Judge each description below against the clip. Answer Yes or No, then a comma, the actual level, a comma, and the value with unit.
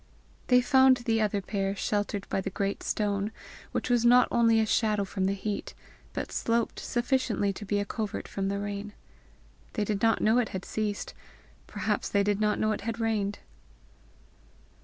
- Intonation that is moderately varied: No, narrow, 2.3 semitones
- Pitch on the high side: Yes, high, 210 Hz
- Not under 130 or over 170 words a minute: No, average, 180 wpm